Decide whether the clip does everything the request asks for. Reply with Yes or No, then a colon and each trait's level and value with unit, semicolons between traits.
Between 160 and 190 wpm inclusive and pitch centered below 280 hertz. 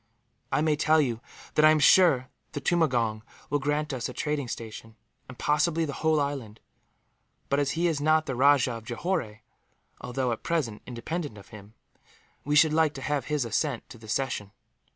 Yes: average, 185 wpm; medium, 140 Hz